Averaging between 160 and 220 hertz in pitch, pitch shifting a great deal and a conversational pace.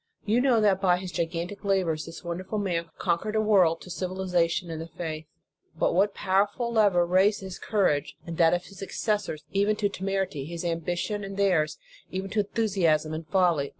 No: medium, 185 Hz; average, 3.2 semitones; average, 185 wpm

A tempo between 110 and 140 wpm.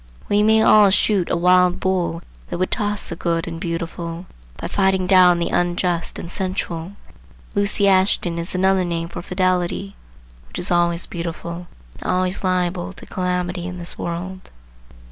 No: average, 160 wpm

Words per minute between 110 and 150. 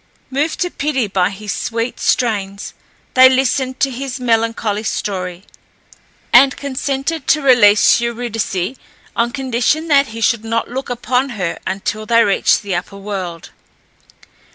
Yes: slow, 135 wpm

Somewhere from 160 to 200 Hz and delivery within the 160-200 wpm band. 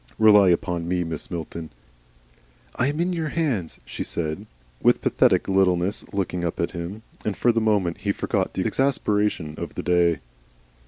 No: very low, 95 Hz; average, 170 wpm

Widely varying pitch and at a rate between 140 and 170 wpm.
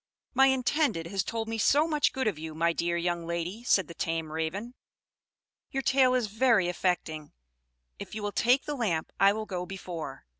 No: wide, 6.4 semitones; average, 190 wpm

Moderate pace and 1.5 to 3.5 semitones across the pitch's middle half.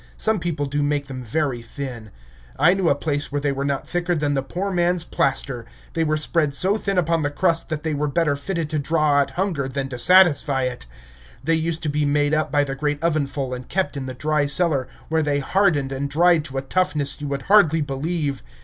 No: fast, 230 wpm; average, 3.1 semitones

